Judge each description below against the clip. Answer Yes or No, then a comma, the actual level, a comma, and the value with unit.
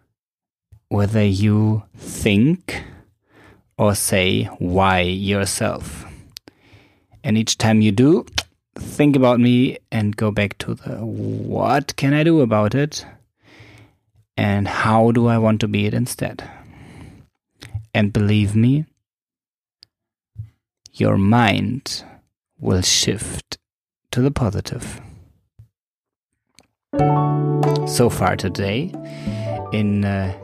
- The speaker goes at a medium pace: No, slow, 100 wpm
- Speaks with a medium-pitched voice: No, low, 105 Hz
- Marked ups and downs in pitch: No, average, 2.9 semitones